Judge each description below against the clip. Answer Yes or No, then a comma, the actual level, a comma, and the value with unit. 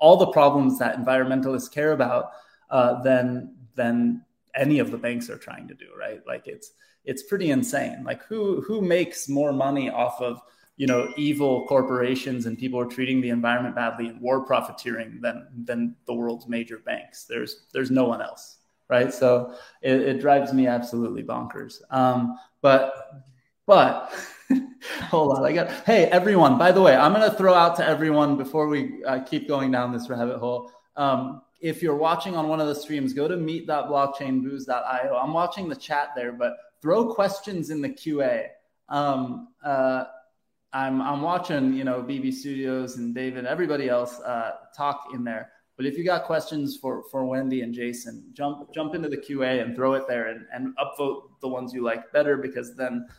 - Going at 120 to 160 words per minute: No, average, 185 wpm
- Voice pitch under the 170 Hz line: Yes, low, 135 Hz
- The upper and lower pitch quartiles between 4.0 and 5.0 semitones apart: No, average, 3.2 semitones